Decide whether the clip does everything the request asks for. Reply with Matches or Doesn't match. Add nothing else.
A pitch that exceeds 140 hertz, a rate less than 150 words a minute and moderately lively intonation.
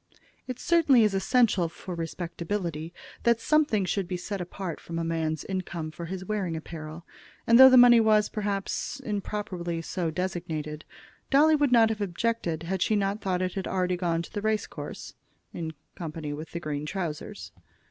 Doesn't match